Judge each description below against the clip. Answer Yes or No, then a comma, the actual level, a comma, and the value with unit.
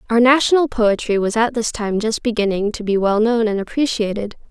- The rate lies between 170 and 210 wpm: Yes, average, 200 wpm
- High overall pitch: Yes, high, 225 Hz